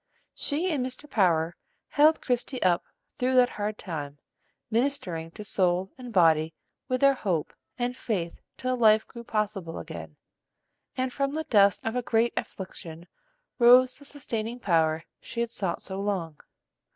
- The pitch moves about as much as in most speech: No, wide, 6.6 semitones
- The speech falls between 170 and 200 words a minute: No, average, 150 wpm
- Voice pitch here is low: No, high, 215 Hz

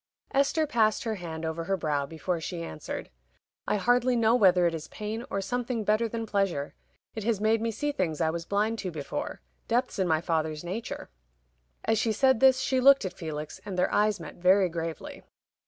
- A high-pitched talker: Yes, high, 200 Hz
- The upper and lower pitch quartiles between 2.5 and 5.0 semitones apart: No, wide, 5.5 semitones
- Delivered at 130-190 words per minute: No, average, 200 wpm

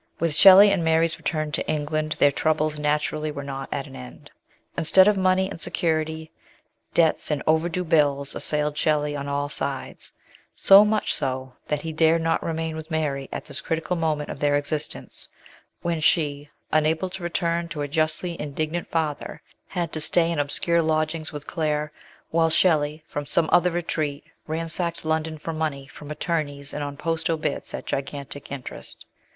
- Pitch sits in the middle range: Yes, medium, 155 Hz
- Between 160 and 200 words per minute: Yes, average, 170 wpm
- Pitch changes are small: Yes, narrow, 2.1 semitones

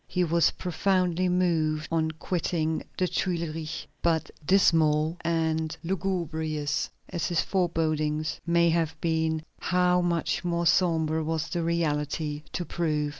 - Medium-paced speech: No, slow, 125 wpm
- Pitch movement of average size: No, narrow, 1.9 semitones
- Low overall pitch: No, medium, 165 Hz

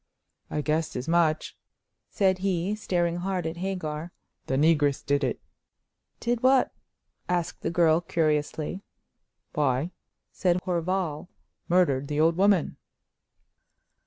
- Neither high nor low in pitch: Yes, medium, 170 Hz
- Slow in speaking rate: Yes, slow, 115 wpm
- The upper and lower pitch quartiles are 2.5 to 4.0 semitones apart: Yes, average, 3.3 semitones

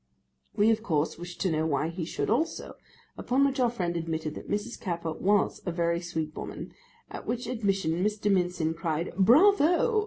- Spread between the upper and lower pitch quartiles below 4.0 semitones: No, wide, 5.5 semitones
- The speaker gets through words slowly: No, average, 180 wpm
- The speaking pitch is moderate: Yes, medium, 180 Hz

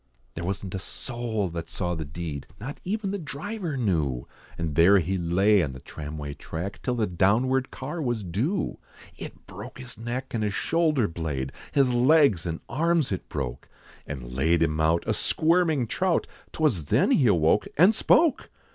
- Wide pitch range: Yes, wide, 8.8 semitones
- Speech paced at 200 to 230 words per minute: No, average, 175 wpm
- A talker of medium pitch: No, low, 105 Hz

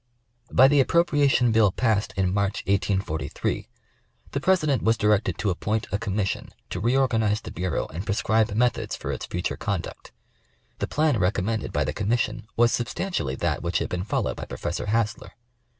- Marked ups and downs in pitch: No, average, 3.8 semitones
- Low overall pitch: Yes, low, 105 Hz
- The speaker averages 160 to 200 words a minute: Yes, average, 170 wpm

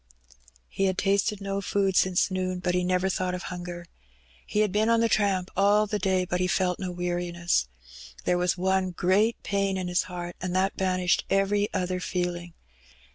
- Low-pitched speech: No, medium, 185 Hz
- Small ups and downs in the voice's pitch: Yes, narrow, 1.7 semitones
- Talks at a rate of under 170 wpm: No, average, 185 wpm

